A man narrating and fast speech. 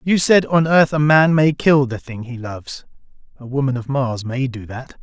Yes: male; fast, 225 wpm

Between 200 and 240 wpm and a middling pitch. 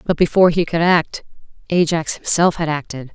No: average, 170 wpm; medium, 170 Hz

